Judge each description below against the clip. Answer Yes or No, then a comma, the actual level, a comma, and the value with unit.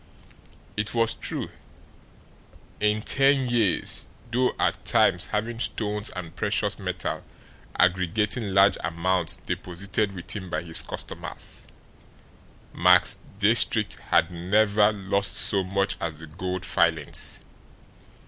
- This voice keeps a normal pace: No, slow, 110 wpm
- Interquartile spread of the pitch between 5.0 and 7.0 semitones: No, average, 2.9 semitones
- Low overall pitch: Yes, low, 100 Hz